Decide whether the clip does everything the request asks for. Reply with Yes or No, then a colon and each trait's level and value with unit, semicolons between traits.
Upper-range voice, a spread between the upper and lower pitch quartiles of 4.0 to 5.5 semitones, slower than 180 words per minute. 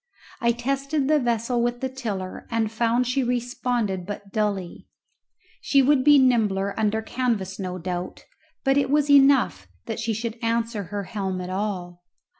Yes: high, 230 Hz; average, 4.3 semitones; average, 160 wpm